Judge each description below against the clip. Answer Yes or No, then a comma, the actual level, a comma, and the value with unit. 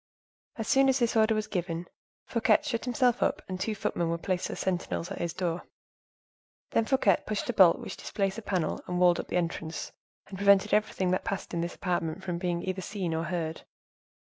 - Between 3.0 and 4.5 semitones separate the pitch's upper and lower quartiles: Yes, average, 3.8 semitones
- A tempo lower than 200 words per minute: No, fast, 205 wpm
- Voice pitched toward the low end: No, medium, 185 Hz